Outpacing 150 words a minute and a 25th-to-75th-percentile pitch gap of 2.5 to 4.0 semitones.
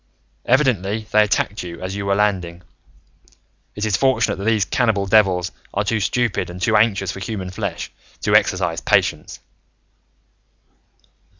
No: average, 140 wpm; average, 2.9 semitones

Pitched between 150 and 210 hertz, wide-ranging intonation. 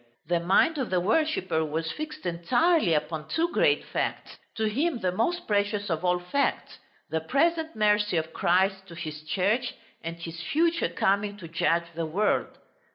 Yes: high, 190 Hz; wide, 7.4 semitones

